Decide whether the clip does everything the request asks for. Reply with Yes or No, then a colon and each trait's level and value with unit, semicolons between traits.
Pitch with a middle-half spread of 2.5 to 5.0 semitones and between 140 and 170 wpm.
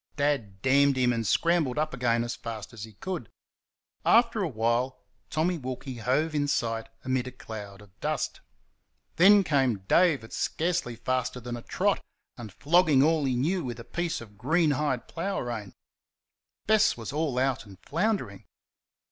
No: wide, 5.4 semitones; average, 165 wpm